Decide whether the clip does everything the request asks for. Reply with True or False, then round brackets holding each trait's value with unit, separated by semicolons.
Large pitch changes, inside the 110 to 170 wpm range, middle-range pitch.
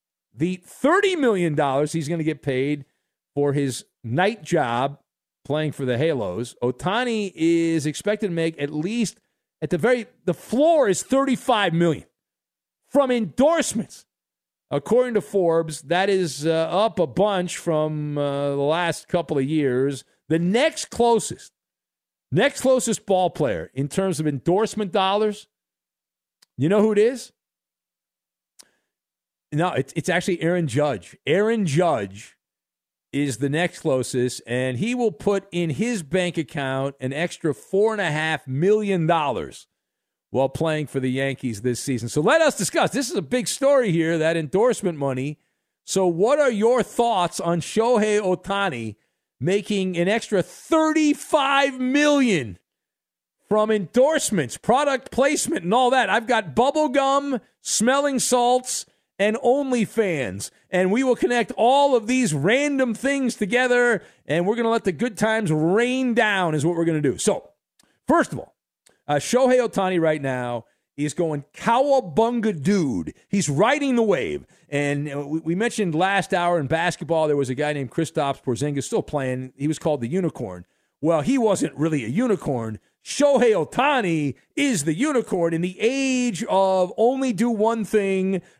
True (7.9 semitones; 155 wpm; 180 Hz)